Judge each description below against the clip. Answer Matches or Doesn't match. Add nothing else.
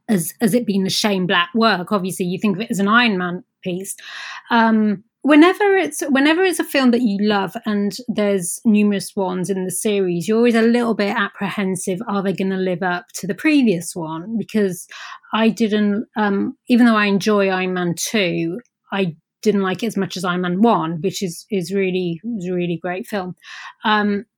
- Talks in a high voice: Matches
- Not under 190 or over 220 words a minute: Matches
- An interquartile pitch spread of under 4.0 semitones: Matches